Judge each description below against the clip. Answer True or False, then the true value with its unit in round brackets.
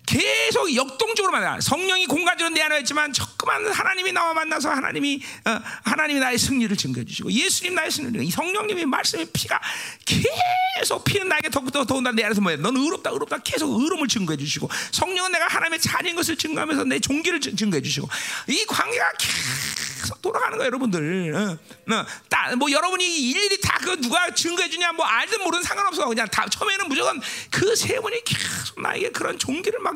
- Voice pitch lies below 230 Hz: False (320 Hz)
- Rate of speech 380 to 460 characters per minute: True (415 characters per minute)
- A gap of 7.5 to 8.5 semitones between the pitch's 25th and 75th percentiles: False (6.2 semitones)